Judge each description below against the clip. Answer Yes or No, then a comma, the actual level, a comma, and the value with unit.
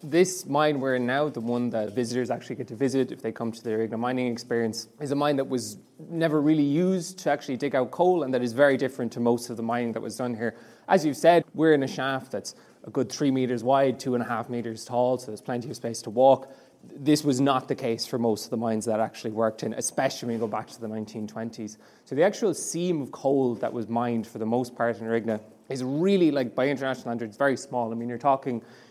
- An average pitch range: Yes, average, 3.2 semitones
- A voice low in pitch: Yes, low, 125 Hz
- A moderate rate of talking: No, fast, 255 wpm